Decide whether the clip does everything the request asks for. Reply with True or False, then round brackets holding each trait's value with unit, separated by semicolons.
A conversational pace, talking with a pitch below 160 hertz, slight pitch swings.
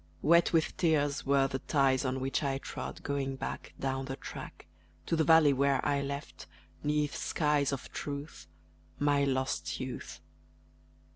True (150 wpm; 140 Hz; 1.6 semitones)